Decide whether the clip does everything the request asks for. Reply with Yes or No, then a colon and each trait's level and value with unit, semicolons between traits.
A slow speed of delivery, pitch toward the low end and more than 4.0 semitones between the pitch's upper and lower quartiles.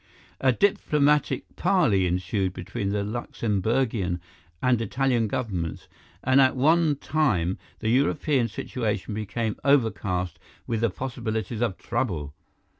Yes: slow, 115 wpm; low, 115 Hz; average, 4.9 semitones